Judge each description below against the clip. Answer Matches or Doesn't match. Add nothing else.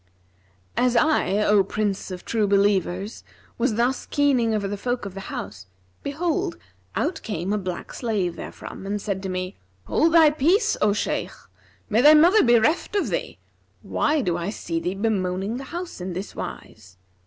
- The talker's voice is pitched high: Matches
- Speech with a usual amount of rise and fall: Doesn't match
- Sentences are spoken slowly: Doesn't match